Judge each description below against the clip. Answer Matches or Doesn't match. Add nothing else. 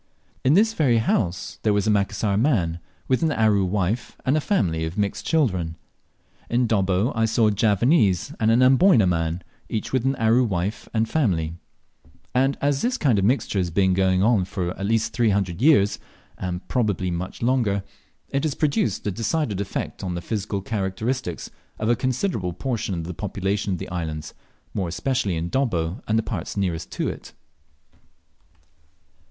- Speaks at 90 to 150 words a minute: Doesn't match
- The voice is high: Doesn't match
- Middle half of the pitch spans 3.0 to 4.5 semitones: Doesn't match